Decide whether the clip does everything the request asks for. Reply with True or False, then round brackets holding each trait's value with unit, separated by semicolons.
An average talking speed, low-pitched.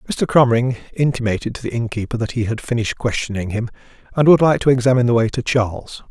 True (195 wpm; 120 Hz)